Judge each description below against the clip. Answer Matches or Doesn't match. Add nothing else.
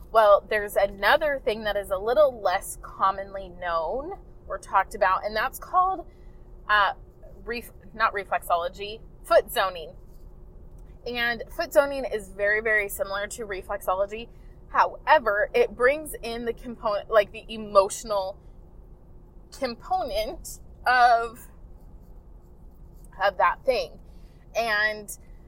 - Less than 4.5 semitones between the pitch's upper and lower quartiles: Matches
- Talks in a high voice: Matches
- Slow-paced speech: Matches